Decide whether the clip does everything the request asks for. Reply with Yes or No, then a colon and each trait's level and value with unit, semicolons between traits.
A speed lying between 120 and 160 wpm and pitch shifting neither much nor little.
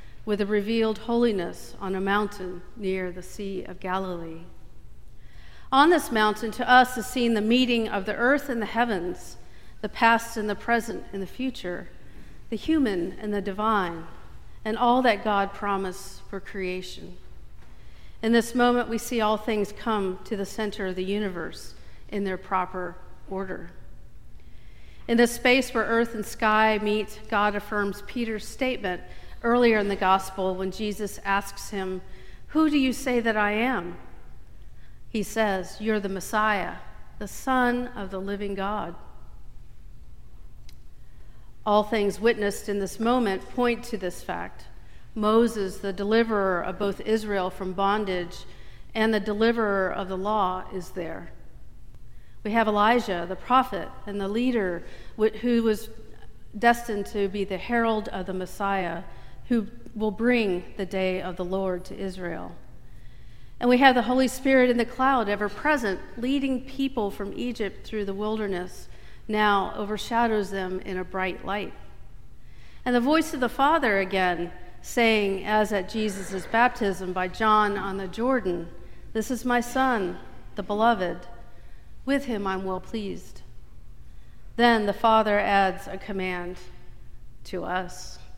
Yes: average, 150 wpm; average, 3.4 semitones